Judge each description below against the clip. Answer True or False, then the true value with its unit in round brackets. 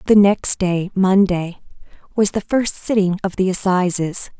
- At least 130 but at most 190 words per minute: True (150 wpm)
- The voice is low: False (190 Hz)